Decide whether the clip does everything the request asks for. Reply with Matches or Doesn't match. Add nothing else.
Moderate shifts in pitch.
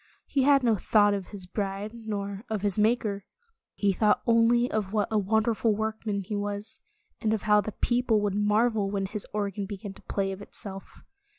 Doesn't match